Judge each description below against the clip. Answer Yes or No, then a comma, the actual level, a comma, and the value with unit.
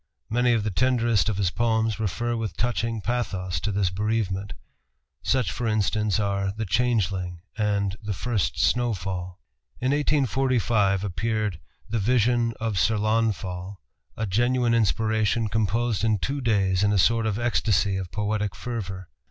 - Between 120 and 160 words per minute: Yes, average, 145 wpm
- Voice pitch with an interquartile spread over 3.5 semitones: No, average, 3.0 semitones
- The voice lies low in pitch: Yes, low, 110 Hz